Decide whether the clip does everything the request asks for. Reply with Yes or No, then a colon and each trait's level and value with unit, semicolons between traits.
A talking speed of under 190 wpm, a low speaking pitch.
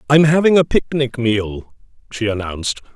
Yes: average, 140 wpm; low, 125 Hz